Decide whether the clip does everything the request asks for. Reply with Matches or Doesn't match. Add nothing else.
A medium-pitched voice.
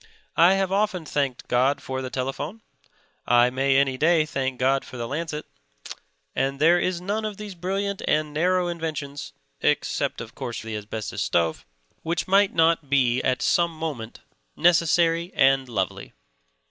Matches